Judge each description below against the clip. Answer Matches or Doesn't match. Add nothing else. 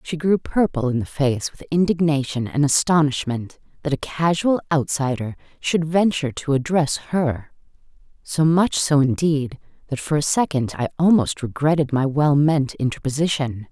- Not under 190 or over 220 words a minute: Doesn't match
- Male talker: Doesn't match